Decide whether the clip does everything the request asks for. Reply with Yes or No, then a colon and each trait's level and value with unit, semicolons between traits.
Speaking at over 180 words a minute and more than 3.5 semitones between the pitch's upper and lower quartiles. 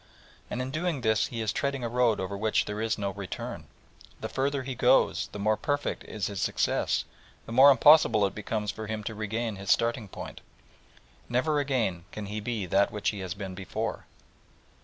Yes: average, 195 wpm; average, 4.0 semitones